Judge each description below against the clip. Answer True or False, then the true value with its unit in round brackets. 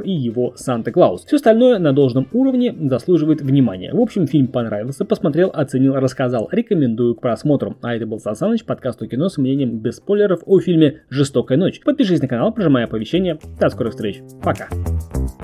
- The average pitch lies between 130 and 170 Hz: True (135 Hz)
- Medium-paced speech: False (180 wpm)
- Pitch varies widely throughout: True (7.0 semitones)